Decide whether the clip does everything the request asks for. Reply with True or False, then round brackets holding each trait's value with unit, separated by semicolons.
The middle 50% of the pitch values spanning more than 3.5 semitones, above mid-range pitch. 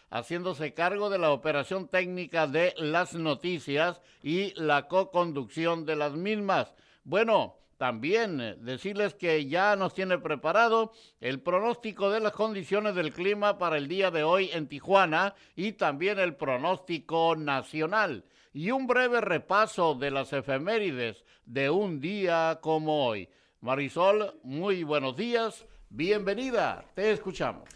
False (4.4 semitones; 175 Hz)